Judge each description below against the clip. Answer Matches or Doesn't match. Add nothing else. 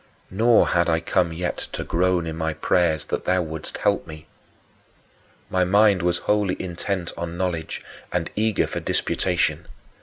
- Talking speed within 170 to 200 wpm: Doesn't match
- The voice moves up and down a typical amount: Doesn't match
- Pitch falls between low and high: Doesn't match